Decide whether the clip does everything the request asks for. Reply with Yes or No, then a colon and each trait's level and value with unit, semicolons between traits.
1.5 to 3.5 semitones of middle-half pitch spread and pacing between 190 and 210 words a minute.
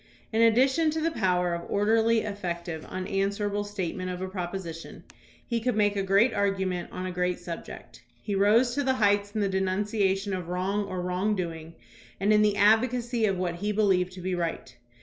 Yes: average, 2.8 semitones; average, 195 wpm